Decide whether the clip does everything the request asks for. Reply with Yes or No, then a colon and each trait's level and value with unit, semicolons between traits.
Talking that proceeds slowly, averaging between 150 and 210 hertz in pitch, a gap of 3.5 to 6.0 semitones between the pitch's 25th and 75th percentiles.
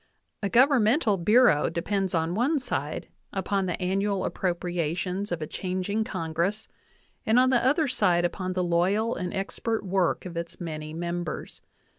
No: average, 155 wpm; medium, 185 Hz; average, 3.8 semitones